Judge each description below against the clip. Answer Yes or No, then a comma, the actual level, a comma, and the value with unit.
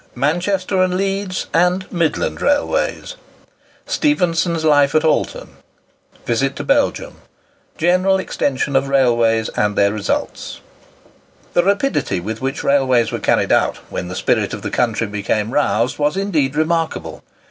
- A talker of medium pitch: Yes, medium, 150 Hz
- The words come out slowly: Yes, slow, 125 wpm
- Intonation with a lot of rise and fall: Yes, wide, 7.2 semitones